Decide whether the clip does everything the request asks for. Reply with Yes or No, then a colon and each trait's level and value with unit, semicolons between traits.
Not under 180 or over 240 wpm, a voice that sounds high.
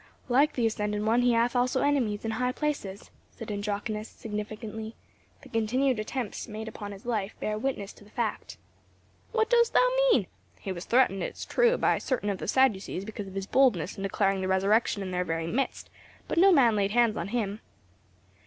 Yes: average, 195 wpm; high, 220 Hz